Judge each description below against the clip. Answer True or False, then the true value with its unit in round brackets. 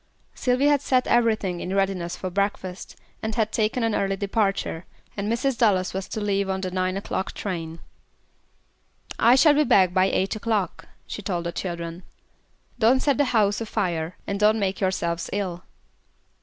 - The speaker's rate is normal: True (170 wpm)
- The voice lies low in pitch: False (200 Hz)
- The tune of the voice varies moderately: True (3.3 semitones)